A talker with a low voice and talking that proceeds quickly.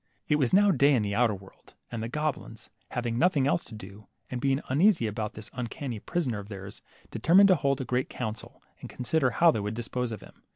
Yes: low, 125 Hz; fast, 225 wpm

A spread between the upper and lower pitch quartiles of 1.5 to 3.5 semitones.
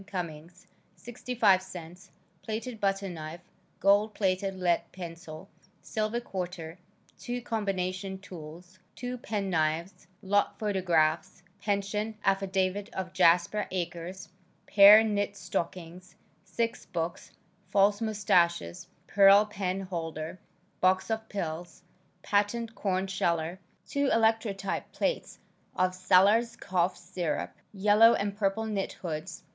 Yes: average, 2.9 semitones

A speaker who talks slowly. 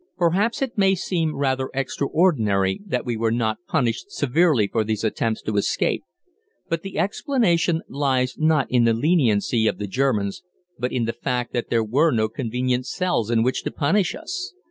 No: average, 175 wpm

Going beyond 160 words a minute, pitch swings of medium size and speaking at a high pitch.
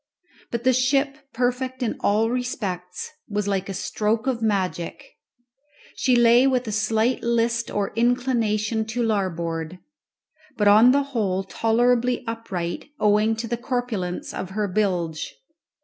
No: slow, 135 wpm; average, 3.5 semitones; high, 225 Hz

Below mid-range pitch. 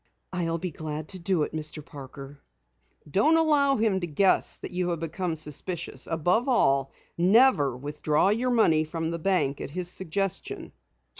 No: medium, 170 Hz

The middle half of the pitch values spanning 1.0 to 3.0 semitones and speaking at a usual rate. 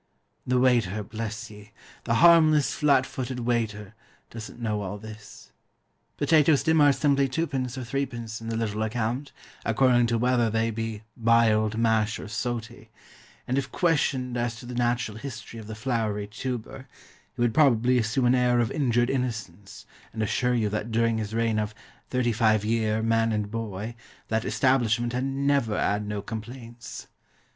Yes: narrow, 2.6 semitones; average, 165 wpm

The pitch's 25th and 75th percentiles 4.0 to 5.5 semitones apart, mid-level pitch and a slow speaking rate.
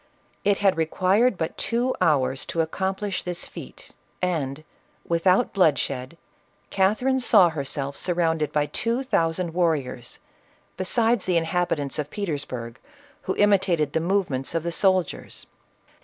Yes: average, 4.5 semitones; medium, 170 Hz; slow, 130 wpm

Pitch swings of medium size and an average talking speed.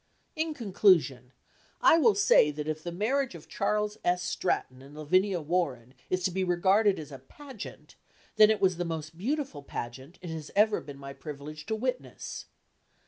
No: wide, 5.9 semitones; average, 175 wpm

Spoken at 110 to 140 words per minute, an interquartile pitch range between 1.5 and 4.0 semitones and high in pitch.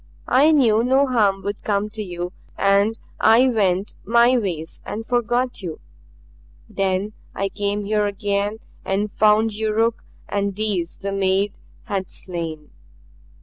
Yes: slow, 135 wpm; narrow, 2.4 semitones; high, 205 Hz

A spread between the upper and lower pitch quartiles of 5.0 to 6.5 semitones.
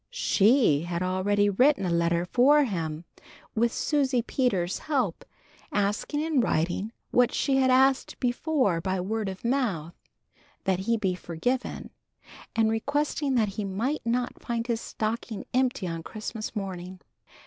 Yes: wide, 5.5 semitones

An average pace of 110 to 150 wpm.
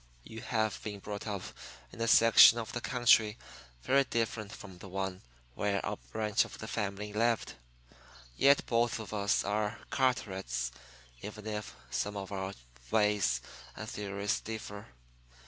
Yes: average, 145 wpm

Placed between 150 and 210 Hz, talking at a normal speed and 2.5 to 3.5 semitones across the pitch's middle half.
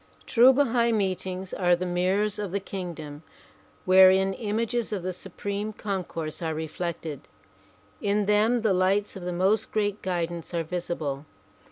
Yes: high, 190 Hz; average, 145 wpm; average, 3.0 semitones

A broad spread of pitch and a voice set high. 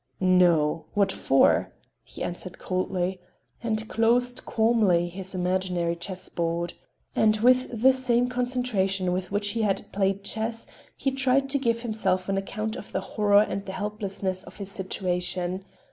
No: average, 3.9 semitones; high, 200 Hz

